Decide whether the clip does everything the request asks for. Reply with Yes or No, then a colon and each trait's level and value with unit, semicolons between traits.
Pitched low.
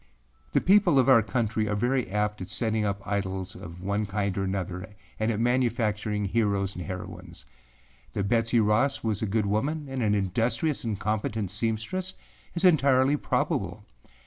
Yes: low, 110 Hz